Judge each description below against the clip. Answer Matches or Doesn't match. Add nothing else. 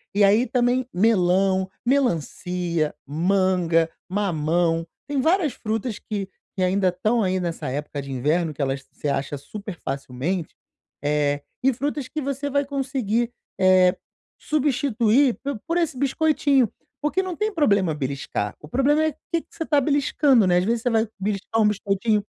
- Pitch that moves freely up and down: Matches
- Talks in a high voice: Matches